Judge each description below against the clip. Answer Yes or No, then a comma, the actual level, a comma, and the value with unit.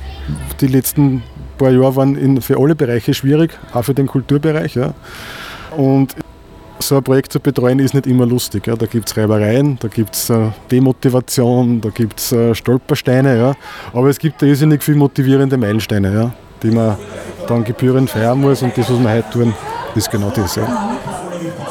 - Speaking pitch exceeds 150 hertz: No, low, 125 Hz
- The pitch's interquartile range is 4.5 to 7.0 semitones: No, average, 3.5 semitones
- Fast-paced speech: No, average, 170 wpm